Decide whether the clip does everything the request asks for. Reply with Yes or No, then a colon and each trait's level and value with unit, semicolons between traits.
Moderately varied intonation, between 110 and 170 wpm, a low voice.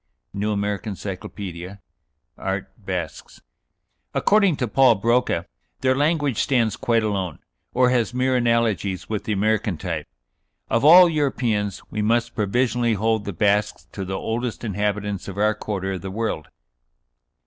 Yes: average, 3.6 semitones; average, 145 wpm; low, 105 Hz